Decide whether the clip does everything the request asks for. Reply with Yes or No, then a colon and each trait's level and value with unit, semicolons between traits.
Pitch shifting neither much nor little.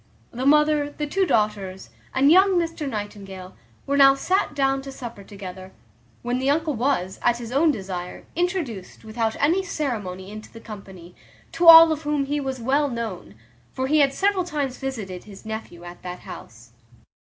No: wide, 6.8 semitones